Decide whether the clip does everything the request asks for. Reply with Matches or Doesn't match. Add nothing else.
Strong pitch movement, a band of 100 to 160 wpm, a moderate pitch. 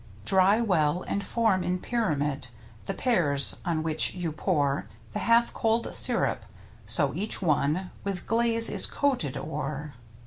Matches